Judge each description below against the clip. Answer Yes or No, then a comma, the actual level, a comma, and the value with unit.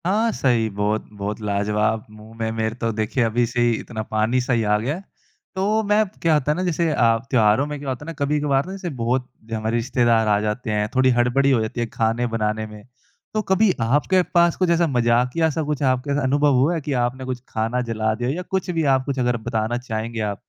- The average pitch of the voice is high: No, low, 125 Hz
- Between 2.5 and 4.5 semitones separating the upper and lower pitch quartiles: No, average, 5.0 semitones